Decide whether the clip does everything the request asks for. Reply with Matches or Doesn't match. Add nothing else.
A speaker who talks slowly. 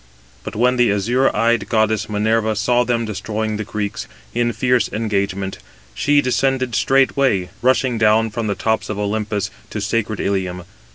Doesn't match